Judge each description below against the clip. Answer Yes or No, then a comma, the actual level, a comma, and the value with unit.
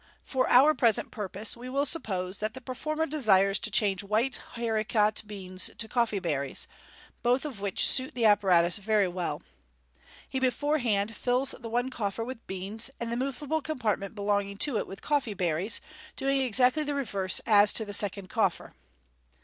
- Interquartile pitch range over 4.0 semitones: Yes, average, 4.5 semitones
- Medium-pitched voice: No, high, 220 Hz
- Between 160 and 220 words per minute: Yes, average, 165 wpm